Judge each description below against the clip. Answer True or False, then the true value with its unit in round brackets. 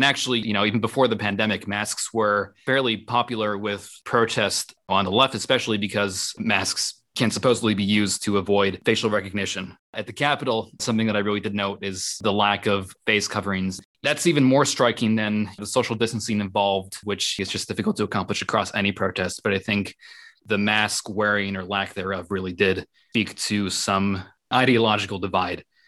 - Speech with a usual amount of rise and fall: False (2.0 semitones)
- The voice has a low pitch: True (105 Hz)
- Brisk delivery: False (180 wpm)